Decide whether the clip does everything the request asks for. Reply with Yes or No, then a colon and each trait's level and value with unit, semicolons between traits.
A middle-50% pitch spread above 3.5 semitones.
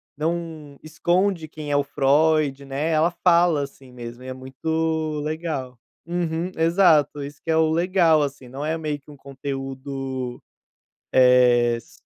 No: average, 3.2 semitones